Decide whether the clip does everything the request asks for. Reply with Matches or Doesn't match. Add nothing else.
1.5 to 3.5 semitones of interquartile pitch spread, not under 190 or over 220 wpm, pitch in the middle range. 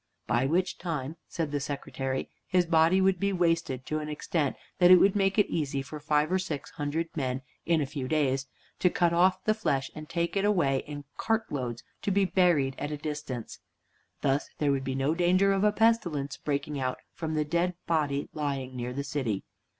Doesn't match